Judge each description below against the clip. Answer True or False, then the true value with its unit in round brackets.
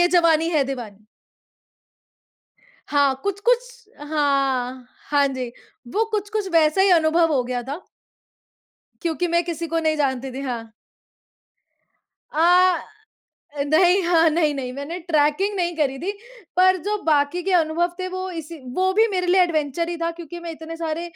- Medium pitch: False (330 Hz)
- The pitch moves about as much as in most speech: True (3.8 semitones)